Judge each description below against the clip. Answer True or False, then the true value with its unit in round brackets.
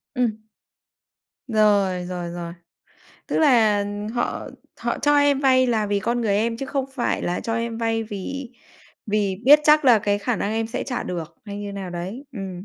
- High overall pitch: True (220 Hz)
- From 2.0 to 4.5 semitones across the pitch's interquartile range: True (3.7 semitones)